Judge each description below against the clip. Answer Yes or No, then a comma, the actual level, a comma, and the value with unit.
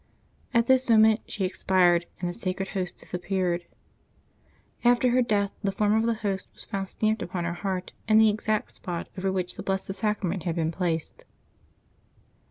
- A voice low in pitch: No, high, 195 Hz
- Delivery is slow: No, average, 175 wpm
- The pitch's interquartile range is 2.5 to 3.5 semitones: Yes, average, 3.2 semitones